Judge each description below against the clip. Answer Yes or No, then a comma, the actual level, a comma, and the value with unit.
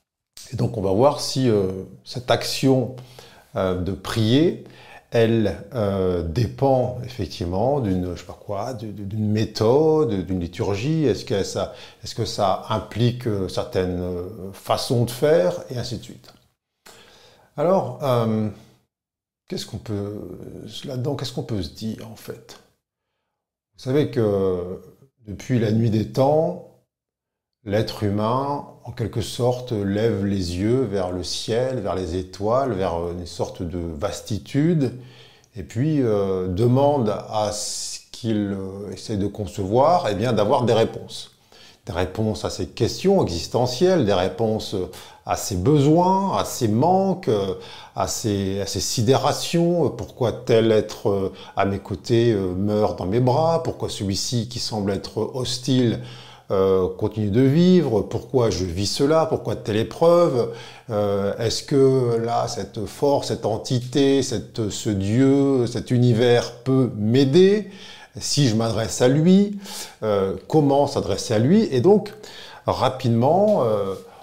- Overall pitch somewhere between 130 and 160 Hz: No, low, 115 Hz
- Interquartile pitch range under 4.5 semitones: No, average, 5.0 semitones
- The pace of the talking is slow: Yes, slow, 140 wpm